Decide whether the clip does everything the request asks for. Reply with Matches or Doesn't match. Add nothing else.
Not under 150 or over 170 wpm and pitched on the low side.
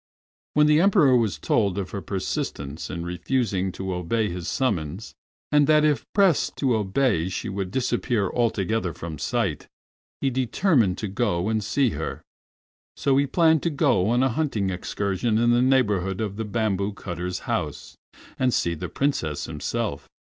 Matches